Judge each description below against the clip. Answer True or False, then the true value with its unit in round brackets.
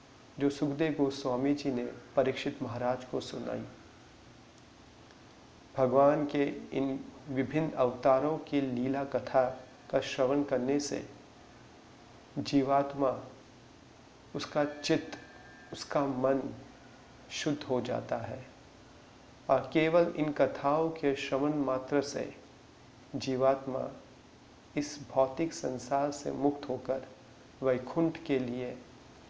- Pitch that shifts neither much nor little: False (1.7 semitones)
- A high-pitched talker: False (135 Hz)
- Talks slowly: True (100 wpm)